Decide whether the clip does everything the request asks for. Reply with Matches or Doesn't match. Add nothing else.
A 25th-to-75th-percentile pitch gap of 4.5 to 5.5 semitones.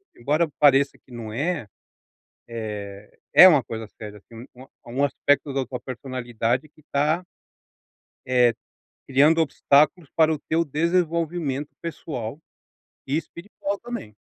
Matches